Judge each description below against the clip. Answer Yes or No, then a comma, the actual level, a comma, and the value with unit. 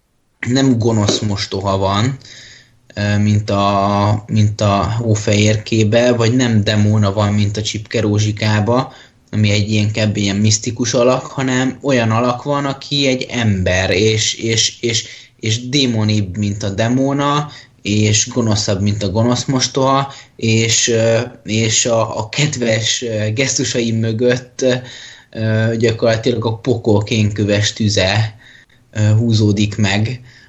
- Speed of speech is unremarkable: Yes, average, 115 wpm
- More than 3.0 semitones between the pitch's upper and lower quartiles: No, average, 2.7 semitones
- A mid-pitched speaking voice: No, low, 115 Hz